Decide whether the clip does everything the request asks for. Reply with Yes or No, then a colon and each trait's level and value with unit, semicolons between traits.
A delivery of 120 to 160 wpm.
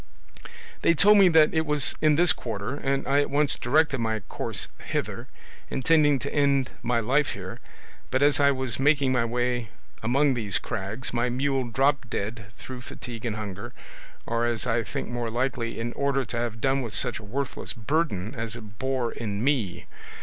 No: average, 185 wpm